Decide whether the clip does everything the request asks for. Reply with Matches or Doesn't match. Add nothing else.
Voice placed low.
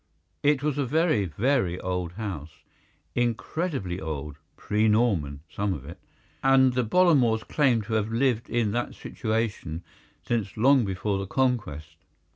Matches